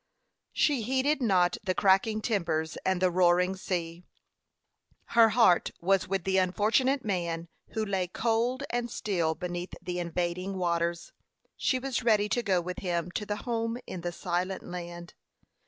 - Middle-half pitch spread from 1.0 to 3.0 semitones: No, average, 4.2 semitones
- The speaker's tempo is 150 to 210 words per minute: Yes, average, 155 wpm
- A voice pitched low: No, medium, 185 Hz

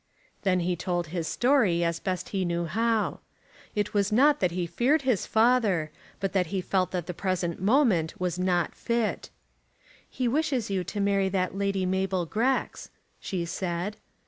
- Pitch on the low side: No, high, 190 Hz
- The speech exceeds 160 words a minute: Yes, average, 170 wpm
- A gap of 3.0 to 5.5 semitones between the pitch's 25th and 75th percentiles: Yes, average, 3.7 semitones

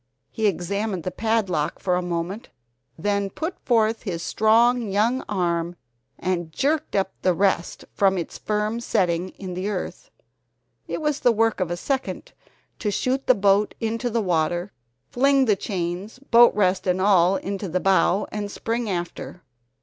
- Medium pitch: No, high, 200 Hz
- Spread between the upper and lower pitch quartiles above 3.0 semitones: Yes, average, 3.9 semitones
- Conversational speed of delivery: Yes, average, 160 wpm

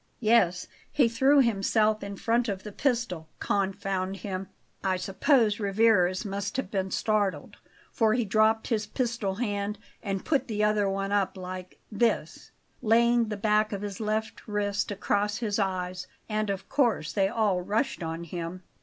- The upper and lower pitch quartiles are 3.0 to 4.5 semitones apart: No, narrow, 2.6 semitones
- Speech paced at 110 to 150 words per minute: No, average, 160 wpm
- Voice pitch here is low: No, high, 205 Hz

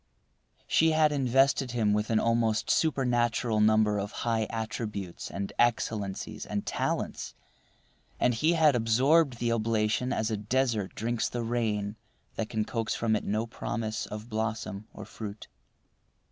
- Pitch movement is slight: Yes, narrow, 2.2 semitones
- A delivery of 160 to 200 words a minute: No, average, 145 wpm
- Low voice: Yes, low, 115 Hz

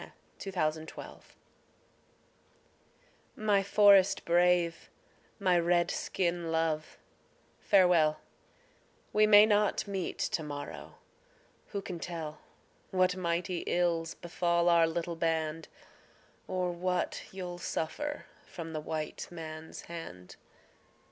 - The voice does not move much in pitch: Yes, narrow, 2.2 semitones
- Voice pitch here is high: No, medium, 170 Hz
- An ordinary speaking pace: No, slow, 110 wpm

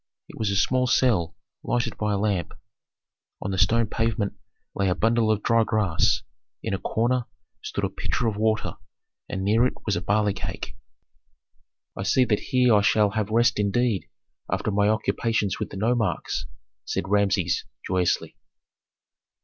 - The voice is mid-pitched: No, low, 105 Hz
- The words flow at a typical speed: Yes, average, 160 wpm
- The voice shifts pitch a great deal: No, average, 2.7 semitones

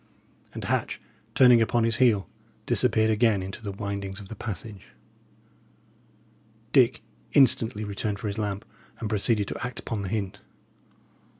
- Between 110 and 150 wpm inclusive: Yes, average, 140 wpm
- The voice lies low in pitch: Yes, low, 105 Hz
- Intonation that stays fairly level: Yes, narrow, 2.2 semitones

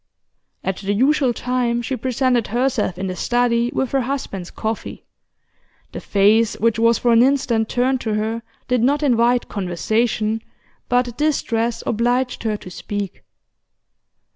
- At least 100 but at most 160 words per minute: Yes, average, 140 wpm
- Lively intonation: No, narrow, 2.5 semitones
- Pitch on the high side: Yes, high, 235 Hz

